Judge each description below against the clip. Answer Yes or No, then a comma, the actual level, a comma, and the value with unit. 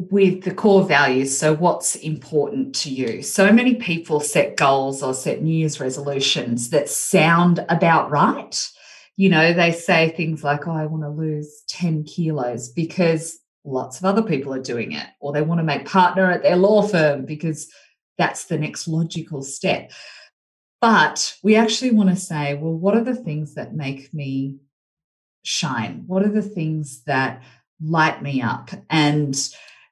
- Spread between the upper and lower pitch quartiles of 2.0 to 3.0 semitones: No, average, 4.3 semitones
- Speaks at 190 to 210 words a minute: No, average, 170 wpm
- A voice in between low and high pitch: Yes, medium, 160 Hz